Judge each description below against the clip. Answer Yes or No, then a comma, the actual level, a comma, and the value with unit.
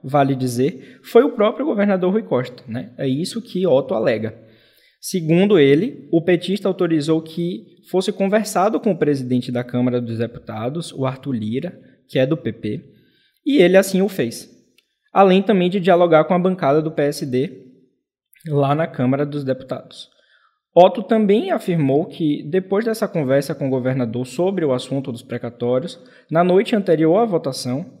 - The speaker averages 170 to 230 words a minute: No, average, 160 wpm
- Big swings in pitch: Yes, wide, 6.2 semitones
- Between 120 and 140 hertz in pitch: No, medium, 155 Hz